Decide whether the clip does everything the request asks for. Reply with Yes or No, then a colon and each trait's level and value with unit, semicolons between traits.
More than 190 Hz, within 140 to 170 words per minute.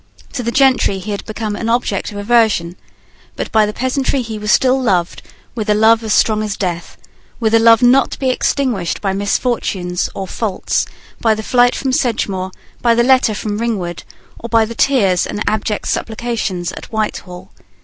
No: high, 220 Hz; average, 180 wpm